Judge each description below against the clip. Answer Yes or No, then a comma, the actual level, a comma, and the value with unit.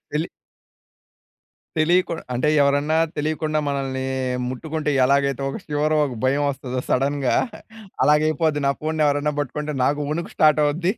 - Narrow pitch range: Yes, narrow, 1.9 semitones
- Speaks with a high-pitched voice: No, medium, 150 Hz